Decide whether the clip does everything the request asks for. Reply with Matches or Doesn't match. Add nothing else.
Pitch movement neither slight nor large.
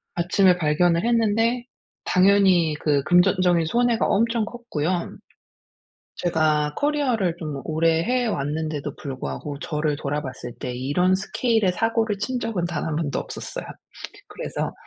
Doesn't match